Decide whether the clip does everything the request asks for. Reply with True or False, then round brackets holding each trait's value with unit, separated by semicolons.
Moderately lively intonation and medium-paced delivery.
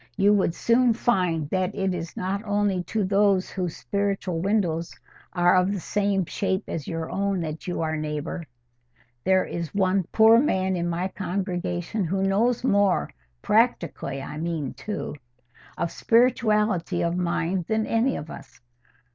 True (3.3 semitones; 145 wpm)